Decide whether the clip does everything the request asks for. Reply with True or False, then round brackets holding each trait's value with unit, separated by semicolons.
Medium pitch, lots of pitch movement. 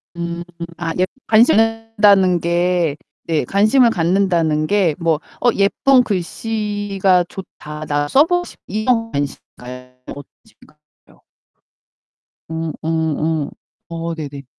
False (175 Hz; 4.8 semitones)